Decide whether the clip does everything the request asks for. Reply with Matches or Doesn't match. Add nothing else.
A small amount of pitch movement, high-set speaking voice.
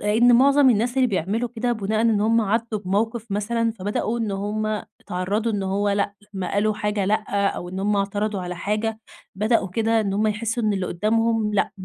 Matches